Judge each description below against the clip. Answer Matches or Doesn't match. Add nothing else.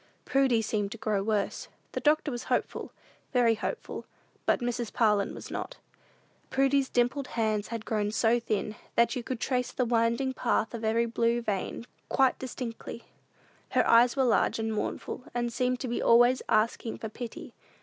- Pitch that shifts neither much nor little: Doesn't match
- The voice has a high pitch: Matches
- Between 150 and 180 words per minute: Matches